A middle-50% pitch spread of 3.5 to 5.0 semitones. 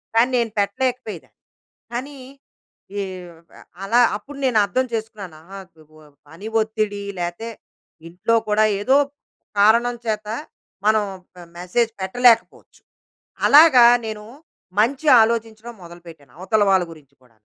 Yes: average, 4.1 semitones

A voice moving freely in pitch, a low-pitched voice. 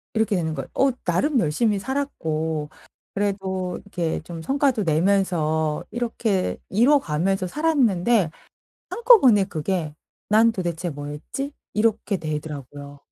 No: wide, 6.2 semitones; high, 190 Hz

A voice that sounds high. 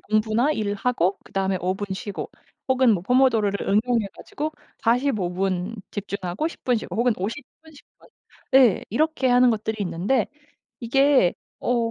Yes: high, 225 Hz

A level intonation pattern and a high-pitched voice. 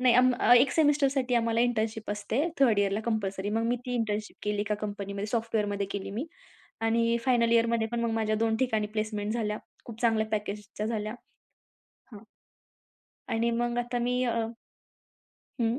Yes: narrow, 2.2 semitones; high, 225 Hz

